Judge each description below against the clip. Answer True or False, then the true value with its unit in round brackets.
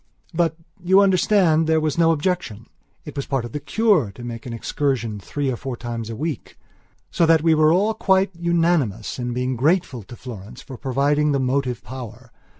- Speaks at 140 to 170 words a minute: False (190 wpm)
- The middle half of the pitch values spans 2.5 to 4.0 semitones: False (5.3 semitones)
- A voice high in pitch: False (140 Hz)